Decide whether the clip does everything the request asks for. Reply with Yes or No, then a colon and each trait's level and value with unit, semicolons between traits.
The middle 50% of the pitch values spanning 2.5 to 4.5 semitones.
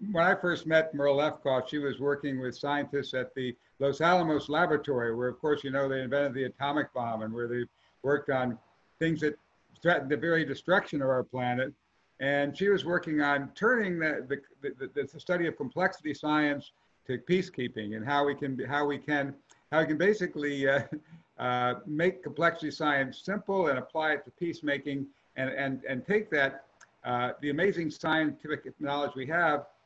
Yes: average, 3.1 semitones